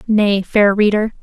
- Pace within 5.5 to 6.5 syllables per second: No, 3.9 syllables/s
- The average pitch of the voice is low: No, high, 205 Hz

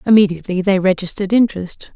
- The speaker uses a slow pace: Yes, slow, 125 wpm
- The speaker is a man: No, female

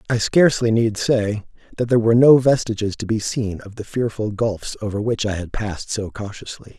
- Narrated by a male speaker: Yes, male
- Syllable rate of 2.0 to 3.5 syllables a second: No, 5.5 syllables/s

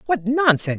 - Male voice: Yes, male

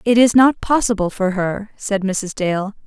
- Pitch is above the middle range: Yes, high, 210 Hz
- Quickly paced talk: No, average, 190 wpm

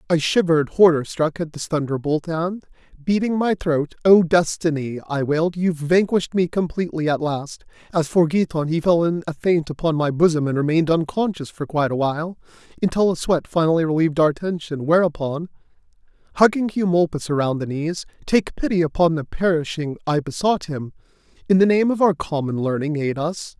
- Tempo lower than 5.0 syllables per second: No, 5.5 syllables/s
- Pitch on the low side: No, medium, 165 Hz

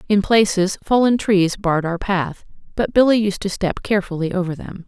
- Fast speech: No, average, 185 wpm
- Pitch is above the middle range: Yes, high, 195 Hz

